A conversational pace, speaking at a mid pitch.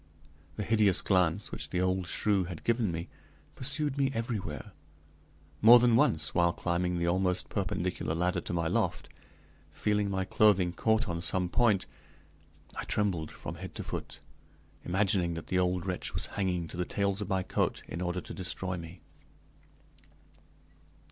No: average, 160 wpm; very low, 95 Hz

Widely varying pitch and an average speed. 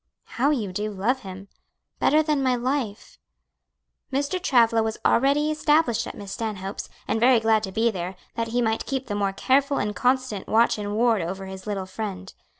No: average, 4.6 semitones; average, 190 wpm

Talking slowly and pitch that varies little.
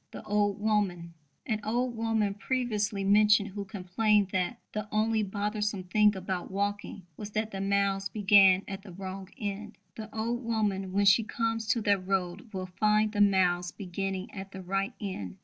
No: average, 170 wpm; narrow, 1.9 semitones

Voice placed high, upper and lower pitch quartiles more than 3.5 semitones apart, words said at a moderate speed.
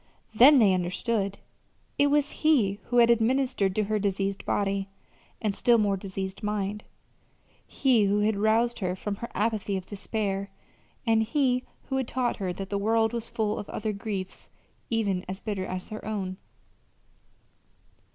No: high, 210 Hz; average, 2.9 semitones; average, 160 wpm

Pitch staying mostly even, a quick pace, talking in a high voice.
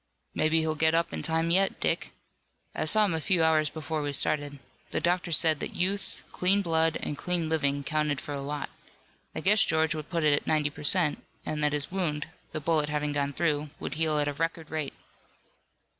No: narrow, 2.1 semitones; fast, 210 wpm; medium, 155 Hz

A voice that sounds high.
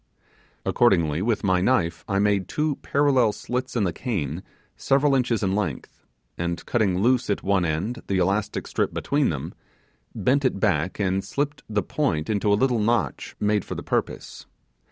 No: low, 105 Hz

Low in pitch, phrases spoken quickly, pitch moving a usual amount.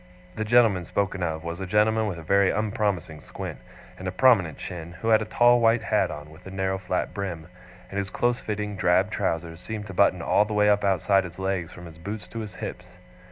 Yes: very low, 95 Hz; fast, 225 wpm; average, 3.1 semitones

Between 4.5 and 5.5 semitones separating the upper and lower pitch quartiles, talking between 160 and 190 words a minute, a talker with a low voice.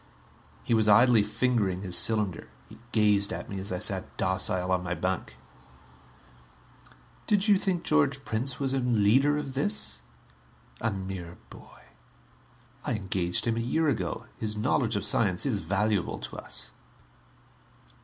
No: average, 5.2 semitones; average, 145 wpm; low, 105 Hz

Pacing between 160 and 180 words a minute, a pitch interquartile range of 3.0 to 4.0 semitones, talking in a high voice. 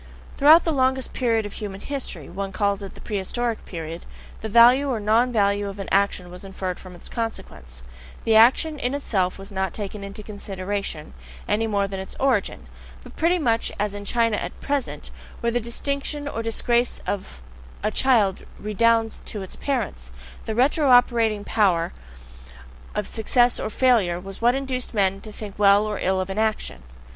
Yes: average, 175 wpm; average, 3.7 semitones; high, 215 Hz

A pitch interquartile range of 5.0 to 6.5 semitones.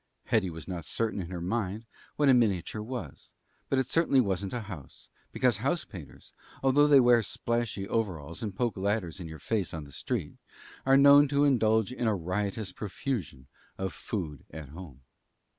Yes: wide, 5.4 semitones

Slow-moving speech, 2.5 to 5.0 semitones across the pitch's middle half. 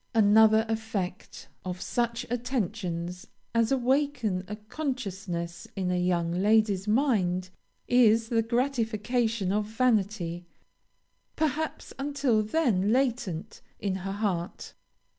Yes: slow, 105 wpm; average, 4.6 semitones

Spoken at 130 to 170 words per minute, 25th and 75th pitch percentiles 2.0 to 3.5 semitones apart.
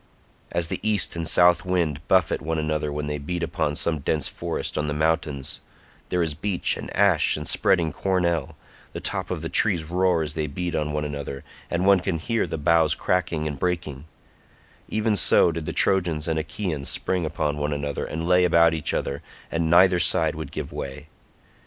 No: average, 190 wpm; average, 2.9 semitones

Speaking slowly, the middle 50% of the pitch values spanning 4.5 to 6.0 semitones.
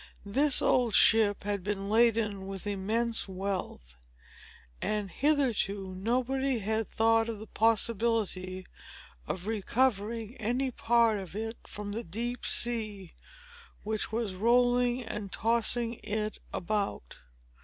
No: slow, 115 wpm; average, 2.8 semitones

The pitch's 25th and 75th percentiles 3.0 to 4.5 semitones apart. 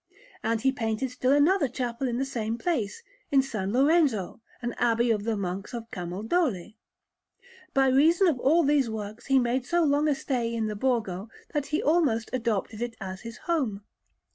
Yes: average, 4.2 semitones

